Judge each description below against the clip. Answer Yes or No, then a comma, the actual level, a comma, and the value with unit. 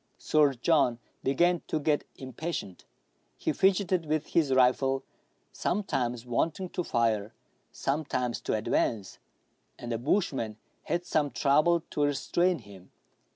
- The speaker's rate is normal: No, slow, 120 wpm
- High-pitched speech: No, medium, 140 Hz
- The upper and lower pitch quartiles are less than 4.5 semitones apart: No, wide, 5.6 semitones